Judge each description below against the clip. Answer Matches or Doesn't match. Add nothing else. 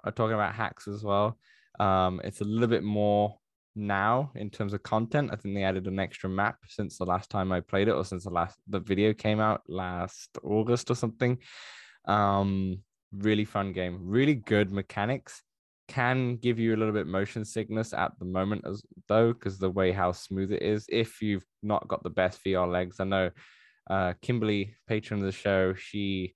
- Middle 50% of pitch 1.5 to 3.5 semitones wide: Matches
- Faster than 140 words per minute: Matches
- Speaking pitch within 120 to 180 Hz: Doesn't match